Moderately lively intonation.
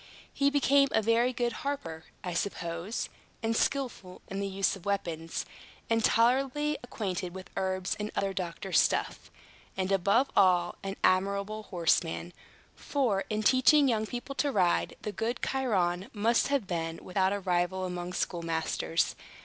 Yes: average, 4.9 semitones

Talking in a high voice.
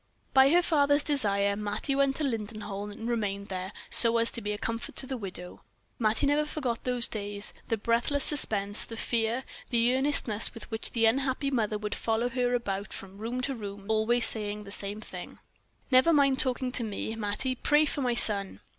Yes: high, 230 Hz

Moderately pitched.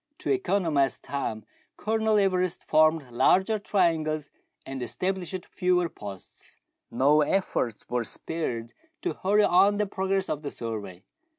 Yes: medium, 165 Hz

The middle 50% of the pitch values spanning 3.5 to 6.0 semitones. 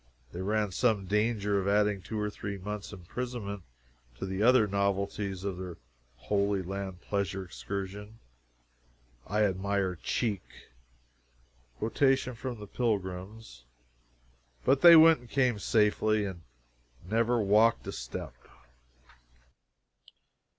No: narrow, 2.5 semitones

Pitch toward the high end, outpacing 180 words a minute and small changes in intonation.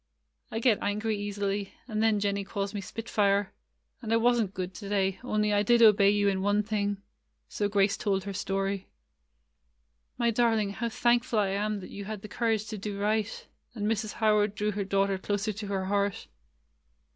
Yes: high, 205 Hz; average, 190 wpm; narrow, 1.5 semitones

